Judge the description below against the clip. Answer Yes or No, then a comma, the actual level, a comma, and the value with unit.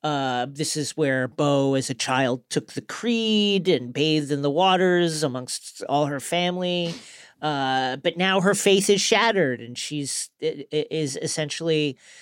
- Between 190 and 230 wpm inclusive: No, average, 160 wpm